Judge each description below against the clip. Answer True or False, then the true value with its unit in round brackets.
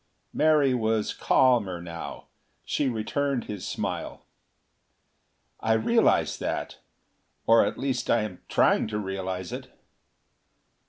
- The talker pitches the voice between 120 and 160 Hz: False (110 Hz)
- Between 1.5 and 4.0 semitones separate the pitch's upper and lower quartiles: False (5.1 semitones)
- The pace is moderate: False (110 wpm)